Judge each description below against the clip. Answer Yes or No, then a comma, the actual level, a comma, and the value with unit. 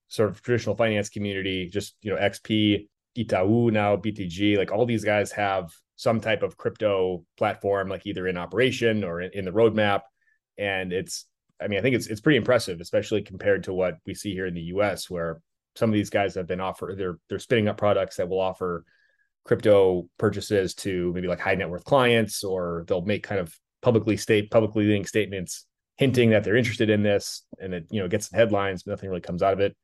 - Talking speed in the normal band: No, fast, 215 wpm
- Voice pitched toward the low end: Yes, low, 100 Hz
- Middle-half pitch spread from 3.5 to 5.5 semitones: No, average, 2.9 semitones